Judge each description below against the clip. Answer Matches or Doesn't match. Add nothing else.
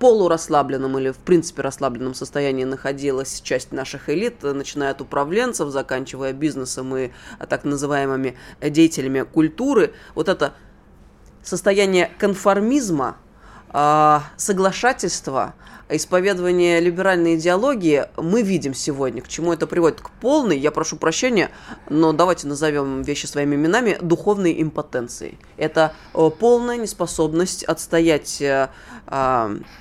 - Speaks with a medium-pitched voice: Matches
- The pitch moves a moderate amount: Matches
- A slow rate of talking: Matches